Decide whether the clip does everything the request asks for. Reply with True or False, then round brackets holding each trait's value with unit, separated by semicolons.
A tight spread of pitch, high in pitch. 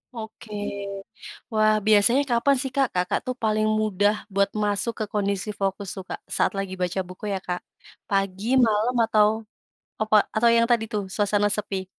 True (2.0 semitones; 210 Hz)